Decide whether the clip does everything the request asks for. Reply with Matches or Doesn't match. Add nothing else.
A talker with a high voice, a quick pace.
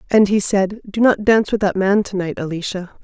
Matches